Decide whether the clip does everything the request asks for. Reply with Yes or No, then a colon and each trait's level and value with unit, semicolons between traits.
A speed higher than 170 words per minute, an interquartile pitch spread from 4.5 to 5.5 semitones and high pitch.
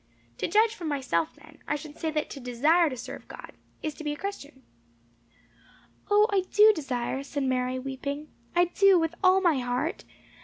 Yes: average, 185 wpm; average, 4.8 semitones; very high, 300 Hz